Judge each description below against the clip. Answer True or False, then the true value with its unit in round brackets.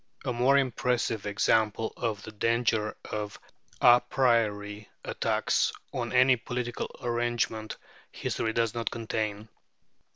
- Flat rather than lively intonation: True (2.1 semitones)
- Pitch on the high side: False (115 Hz)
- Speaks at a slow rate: True (110 wpm)